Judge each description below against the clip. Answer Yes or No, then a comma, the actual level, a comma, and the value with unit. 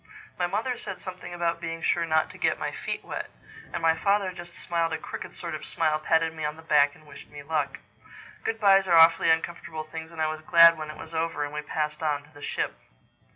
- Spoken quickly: Yes, fast, 240 wpm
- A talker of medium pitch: Yes, medium, 160 Hz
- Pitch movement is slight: Yes, narrow, 1.7 semitones